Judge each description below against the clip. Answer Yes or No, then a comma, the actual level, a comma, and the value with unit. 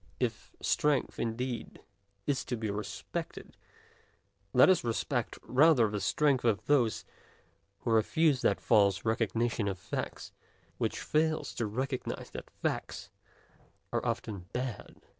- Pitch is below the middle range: Yes, low, 120 Hz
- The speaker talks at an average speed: No, slow, 120 wpm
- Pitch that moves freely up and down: No, average, 3.9 semitones